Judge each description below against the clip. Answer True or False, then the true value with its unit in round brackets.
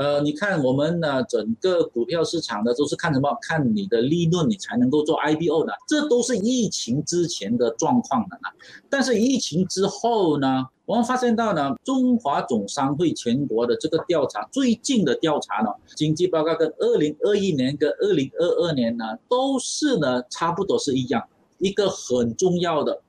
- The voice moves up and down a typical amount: False (8.2 semitones)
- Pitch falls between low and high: True (175 Hz)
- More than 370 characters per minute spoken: False (280 characters per minute)